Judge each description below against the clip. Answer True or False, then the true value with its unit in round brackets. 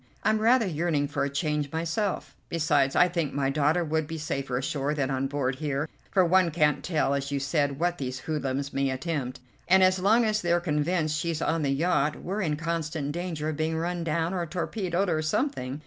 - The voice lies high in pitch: False (155 Hz)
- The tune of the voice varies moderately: True (3.5 semitones)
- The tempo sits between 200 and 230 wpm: True (205 wpm)